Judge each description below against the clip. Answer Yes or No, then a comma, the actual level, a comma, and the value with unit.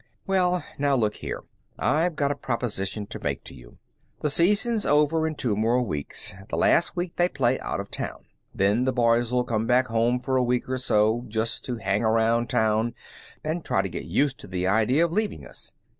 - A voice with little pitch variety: No, average, 5.0 semitones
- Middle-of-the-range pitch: No, low, 125 Hz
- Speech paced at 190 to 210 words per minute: Yes, average, 200 wpm